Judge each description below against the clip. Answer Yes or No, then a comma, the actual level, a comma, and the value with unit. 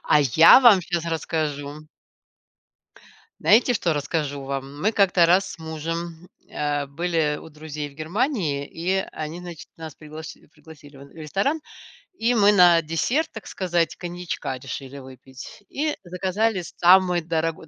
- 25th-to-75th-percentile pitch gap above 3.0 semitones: Yes, average, 3.6 semitones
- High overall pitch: No, medium, 165 Hz